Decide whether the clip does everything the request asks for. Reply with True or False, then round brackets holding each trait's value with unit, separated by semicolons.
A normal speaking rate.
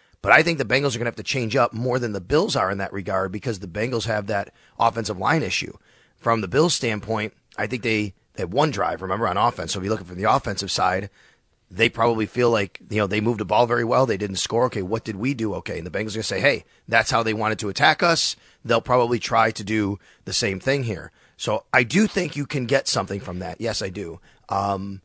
False (260 wpm)